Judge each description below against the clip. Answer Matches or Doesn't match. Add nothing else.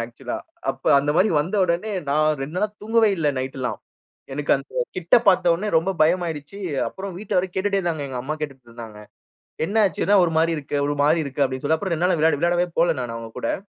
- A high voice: Doesn't match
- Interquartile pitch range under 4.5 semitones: Doesn't match